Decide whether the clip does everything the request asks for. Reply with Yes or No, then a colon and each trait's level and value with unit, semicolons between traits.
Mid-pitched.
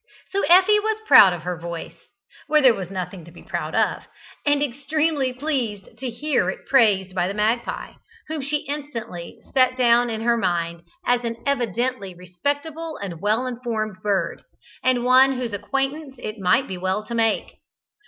No: high, 235 Hz